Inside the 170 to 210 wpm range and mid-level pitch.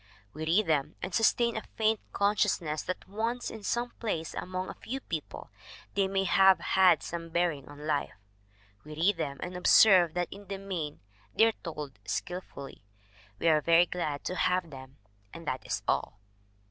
Yes: average, 175 wpm; medium, 175 Hz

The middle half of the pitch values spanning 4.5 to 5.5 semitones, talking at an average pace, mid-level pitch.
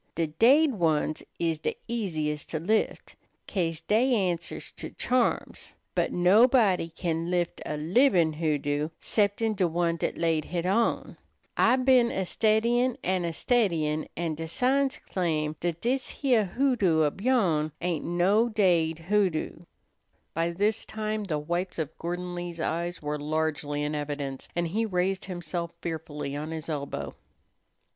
Yes: average, 5.1 semitones; average, 150 wpm; medium, 175 Hz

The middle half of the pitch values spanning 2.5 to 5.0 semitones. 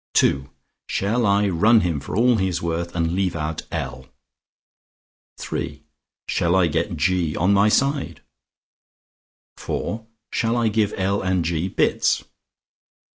Yes: average, 3.9 semitones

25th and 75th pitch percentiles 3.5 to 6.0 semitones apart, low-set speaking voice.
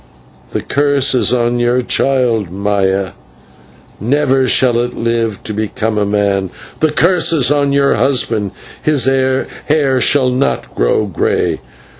Yes: average, 4.5 semitones; low, 125 Hz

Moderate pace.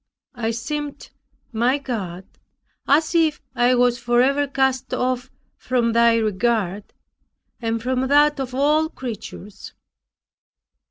No: slow, 110 wpm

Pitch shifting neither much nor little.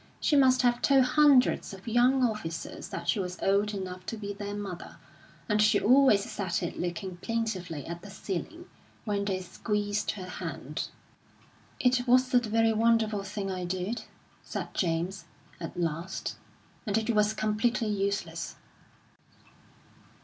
Yes: average, 3.8 semitones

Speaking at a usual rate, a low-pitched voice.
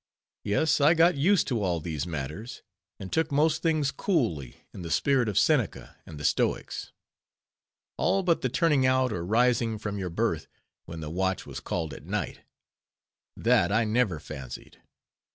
Yes: average, 160 wpm; low, 110 Hz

